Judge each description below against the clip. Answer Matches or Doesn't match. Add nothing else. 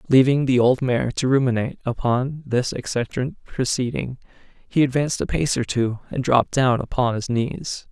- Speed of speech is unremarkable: Matches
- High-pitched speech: Doesn't match